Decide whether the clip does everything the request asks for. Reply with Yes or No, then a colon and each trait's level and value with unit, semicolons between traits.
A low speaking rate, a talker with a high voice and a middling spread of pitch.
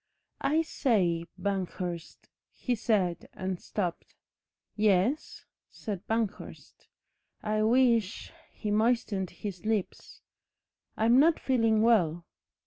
Yes: slow, 100 wpm; high, 215 Hz; average, 3.9 semitones